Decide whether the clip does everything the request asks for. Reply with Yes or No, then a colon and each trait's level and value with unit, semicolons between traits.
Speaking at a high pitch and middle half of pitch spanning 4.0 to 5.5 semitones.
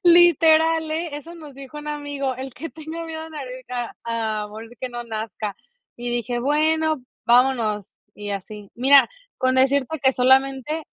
Yes: very high, 270 Hz; average, 4.5 semitones